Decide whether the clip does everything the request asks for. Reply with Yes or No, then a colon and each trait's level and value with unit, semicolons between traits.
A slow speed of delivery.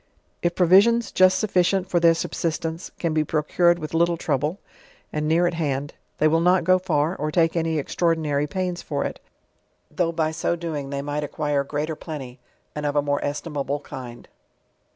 No: average, 190 wpm